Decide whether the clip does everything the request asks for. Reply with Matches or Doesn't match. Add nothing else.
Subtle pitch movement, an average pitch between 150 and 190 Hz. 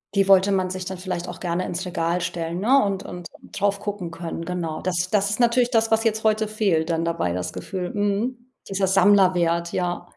Doesn't match